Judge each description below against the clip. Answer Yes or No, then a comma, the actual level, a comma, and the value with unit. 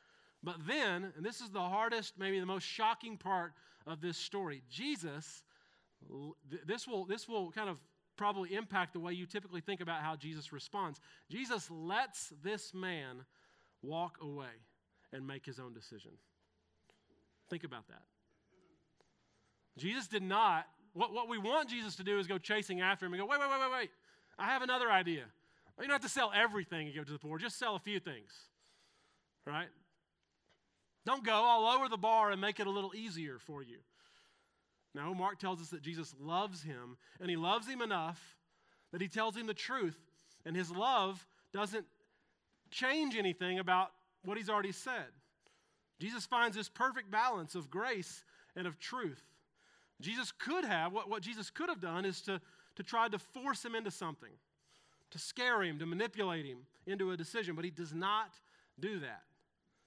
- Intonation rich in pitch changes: No, average, 4.9 semitones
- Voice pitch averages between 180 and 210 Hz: Yes, high, 190 Hz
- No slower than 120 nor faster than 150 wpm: No, average, 180 wpm